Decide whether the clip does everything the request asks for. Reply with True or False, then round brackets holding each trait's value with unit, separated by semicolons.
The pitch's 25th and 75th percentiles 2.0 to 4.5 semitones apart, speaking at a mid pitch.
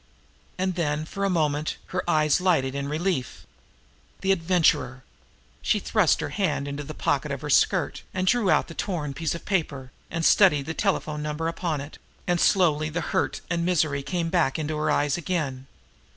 True (3.3 semitones; 160 Hz)